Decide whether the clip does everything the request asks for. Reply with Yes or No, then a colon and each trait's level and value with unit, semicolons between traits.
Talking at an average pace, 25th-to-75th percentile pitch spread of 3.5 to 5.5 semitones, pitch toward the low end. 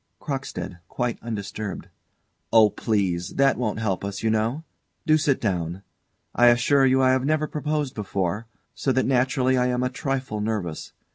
Yes: average, 160 wpm; average, 4.2 semitones; low, 120 Hz